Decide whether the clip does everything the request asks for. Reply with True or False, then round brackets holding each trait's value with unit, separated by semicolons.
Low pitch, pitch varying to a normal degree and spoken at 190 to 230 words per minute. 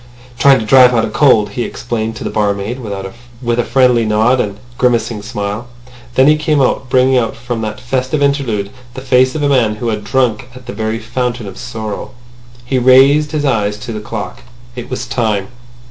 True (120 Hz; 3.1 semitones; 200 wpm)